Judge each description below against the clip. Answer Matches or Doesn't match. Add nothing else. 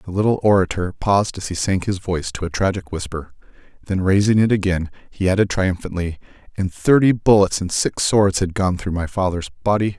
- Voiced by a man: Matches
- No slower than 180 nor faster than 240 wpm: Matches